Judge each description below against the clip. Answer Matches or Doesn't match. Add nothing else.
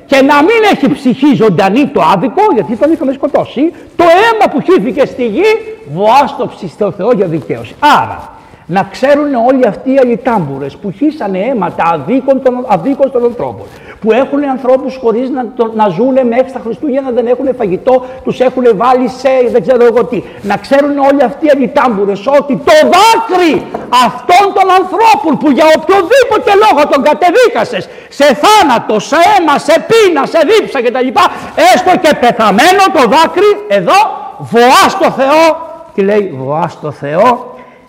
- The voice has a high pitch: Matches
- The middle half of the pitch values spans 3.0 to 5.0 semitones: Doesn't match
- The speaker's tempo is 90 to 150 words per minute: Doesn't match